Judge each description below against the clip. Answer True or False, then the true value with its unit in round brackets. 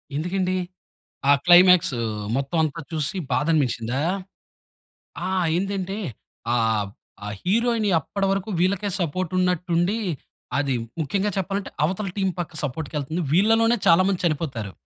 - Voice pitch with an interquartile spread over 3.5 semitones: True (4.8 semitones)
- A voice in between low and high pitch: True (175 Hz)